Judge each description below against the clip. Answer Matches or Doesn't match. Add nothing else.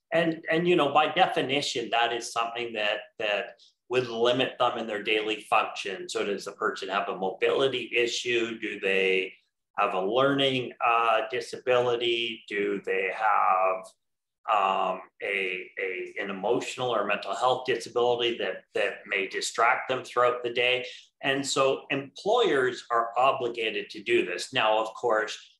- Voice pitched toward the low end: Matches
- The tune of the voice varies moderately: Doesn't match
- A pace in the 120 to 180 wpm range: Matches